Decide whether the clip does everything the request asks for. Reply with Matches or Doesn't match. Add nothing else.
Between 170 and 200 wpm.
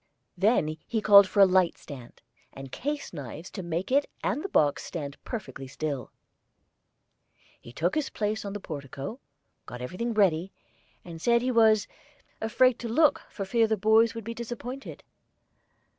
Doesn't match